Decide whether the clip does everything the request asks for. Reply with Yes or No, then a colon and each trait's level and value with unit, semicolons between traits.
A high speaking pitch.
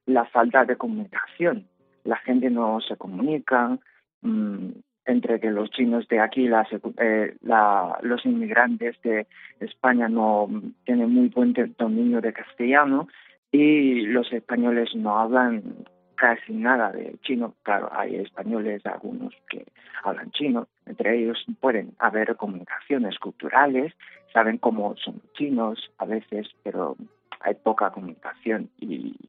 No: low, 120 Hz